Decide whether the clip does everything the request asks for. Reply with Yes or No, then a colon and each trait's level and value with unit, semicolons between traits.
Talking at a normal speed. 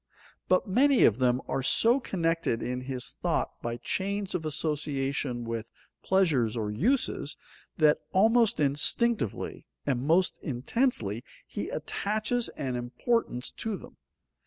No: slow, 125 wpm